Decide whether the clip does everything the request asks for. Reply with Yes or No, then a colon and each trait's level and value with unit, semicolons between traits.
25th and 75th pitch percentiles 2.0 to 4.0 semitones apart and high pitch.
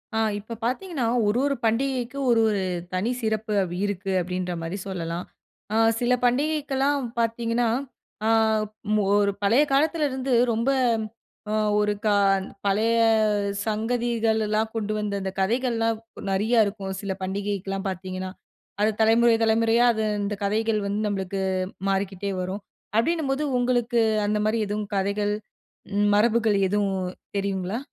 Yes: average, 3.1 semitones; high, 220 Hz